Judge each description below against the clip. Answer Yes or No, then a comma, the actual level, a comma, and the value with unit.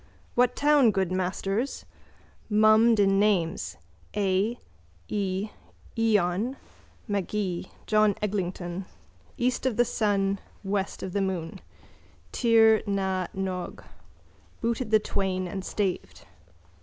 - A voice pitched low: No, high, 200 Hz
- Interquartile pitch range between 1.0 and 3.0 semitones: Yes, average, 2.7 semitones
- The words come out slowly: Yes, slow, 105 wpm